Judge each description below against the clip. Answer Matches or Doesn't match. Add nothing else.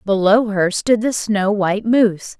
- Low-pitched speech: Doesn't match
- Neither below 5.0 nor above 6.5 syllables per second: Doesn't match